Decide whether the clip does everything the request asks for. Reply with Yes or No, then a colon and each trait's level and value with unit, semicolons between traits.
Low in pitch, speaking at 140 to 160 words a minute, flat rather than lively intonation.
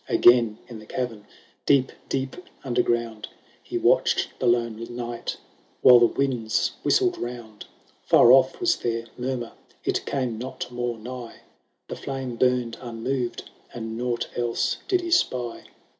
Yes: low, 120 Hz; average, 145 wpm; narrow, 1.7 semitones